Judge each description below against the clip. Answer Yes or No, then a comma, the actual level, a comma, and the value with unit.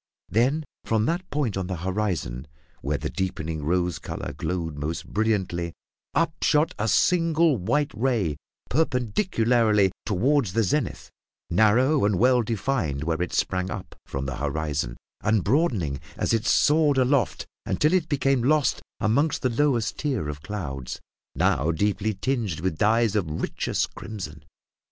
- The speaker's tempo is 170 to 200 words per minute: No, average, 140 wpm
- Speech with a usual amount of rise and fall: No, wide, 7.8 semitones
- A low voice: Yes, low, 105 Hz